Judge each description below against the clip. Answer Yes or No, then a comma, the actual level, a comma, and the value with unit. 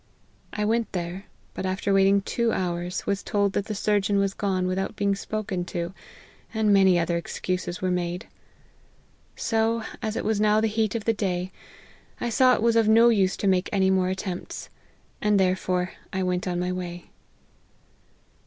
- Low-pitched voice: No, high, 195 Hz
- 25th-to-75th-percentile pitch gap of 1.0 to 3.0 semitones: Yes, average, 2.7 semitones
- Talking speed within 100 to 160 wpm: No, average, 175 wpm